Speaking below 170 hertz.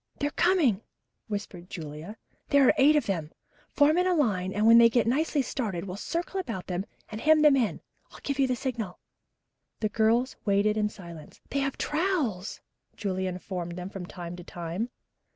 No: high, 220 Hz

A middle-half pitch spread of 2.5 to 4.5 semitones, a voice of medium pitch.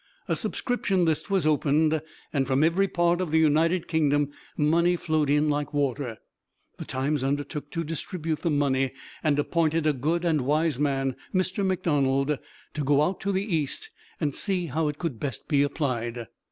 Yes: average, 2.9 semitones; medium, 150 Hz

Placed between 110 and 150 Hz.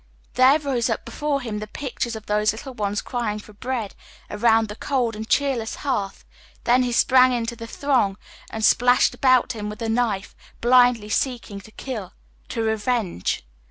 No: high, 230 Hz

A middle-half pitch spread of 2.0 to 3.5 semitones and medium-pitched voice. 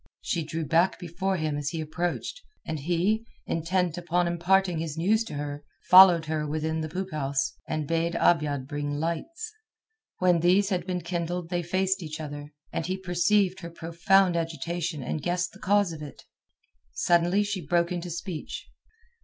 Yes: average, 2.7 semitones; medium, 170 Hz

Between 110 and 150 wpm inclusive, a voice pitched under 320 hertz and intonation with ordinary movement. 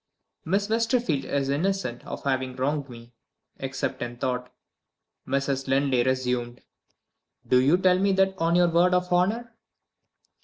No: average, 140 wpm; medium, 140 Hz; wide, 5.9 semitones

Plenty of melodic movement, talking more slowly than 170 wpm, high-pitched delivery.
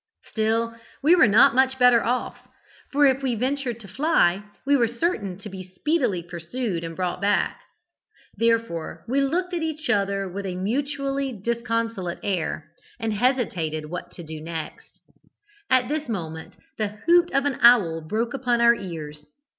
Yes: wide, 6.3 semitones; average, 160 wpm; high, 230 Hz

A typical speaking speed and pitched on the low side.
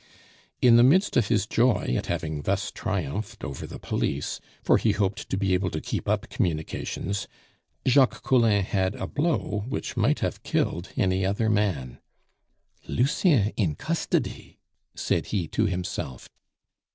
Yes: average, 150 wpm; low, 100 Hz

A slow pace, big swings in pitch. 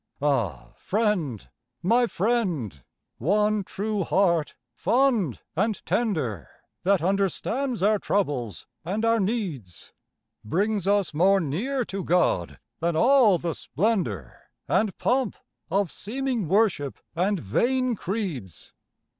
Yes: slow, 110 wpm; wide, 6.0 semitones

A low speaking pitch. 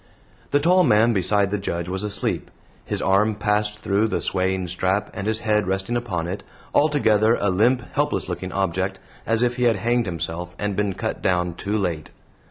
Yes: low, 100 Hz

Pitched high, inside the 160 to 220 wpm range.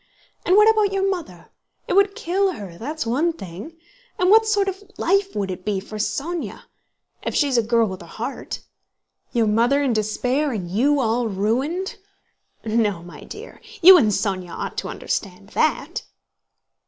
Yes: very high, 255 Hz; average, 165 wpm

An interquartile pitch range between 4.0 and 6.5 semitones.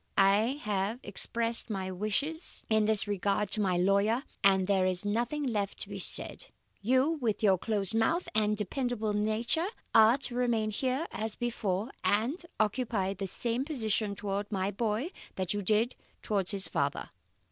No: average, 3.3 semitones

